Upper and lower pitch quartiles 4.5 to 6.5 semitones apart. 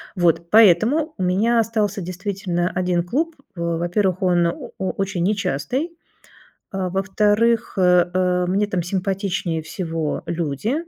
No: average, 3.1 semitones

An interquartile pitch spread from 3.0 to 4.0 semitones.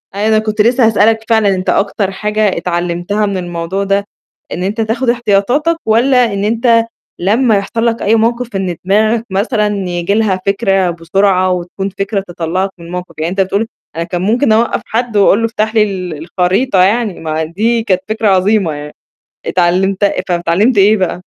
Yes: average, 3.3 semitones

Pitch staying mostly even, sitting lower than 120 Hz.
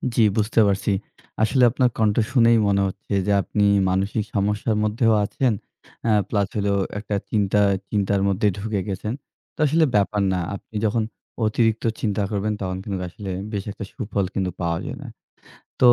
Yes: narrow, 2.0 semitones; low, 105 Hz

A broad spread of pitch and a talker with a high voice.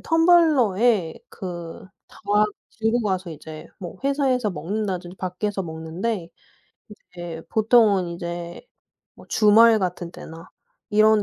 No: average, 4.4 semitones; high, 195 Hz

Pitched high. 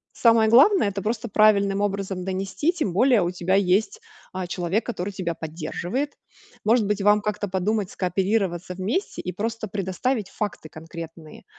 Yes: high, 200 Hz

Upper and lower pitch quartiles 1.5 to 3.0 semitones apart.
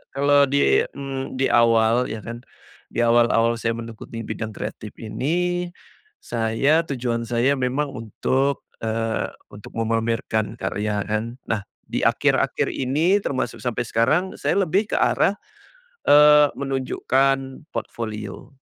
No: average, 3.6 semitones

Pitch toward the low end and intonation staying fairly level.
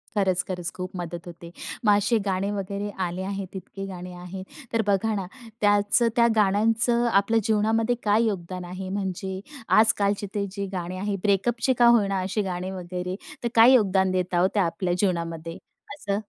No: high, 195 Hz; narrow, 2.3 semitones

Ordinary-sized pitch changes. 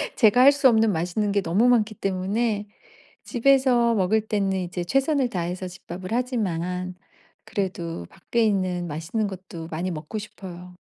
Yes: average, 4.3 semitones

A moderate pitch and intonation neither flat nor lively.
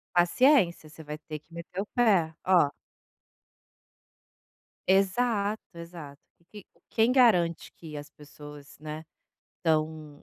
Yes: medium, 170 Hz; average, 4.5 semitones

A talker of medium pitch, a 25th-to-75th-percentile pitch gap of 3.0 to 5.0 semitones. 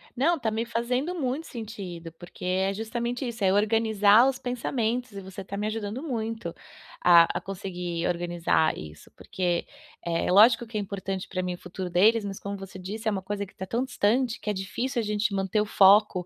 No: high, 205 Hz; average, 3.6 semitones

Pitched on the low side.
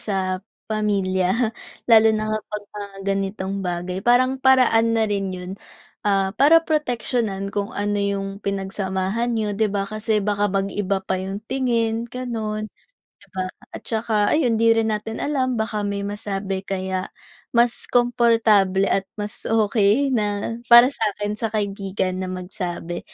No: high, 210 Hz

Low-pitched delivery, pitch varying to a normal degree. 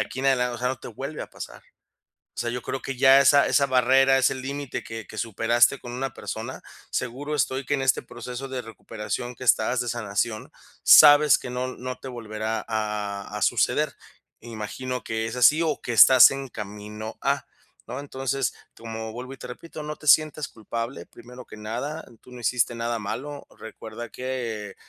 Yes: low, 125 Hz; average, 3.0 semitones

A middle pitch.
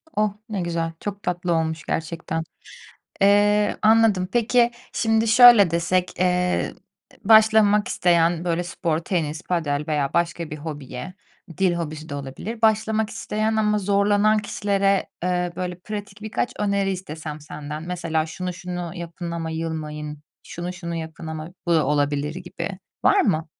Yes: medium, 180 Hz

